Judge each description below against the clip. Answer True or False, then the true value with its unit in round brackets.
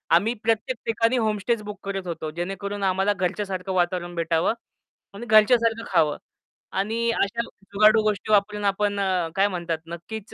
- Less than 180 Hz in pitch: False (200 Hz)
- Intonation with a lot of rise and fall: False (2.8 semitones)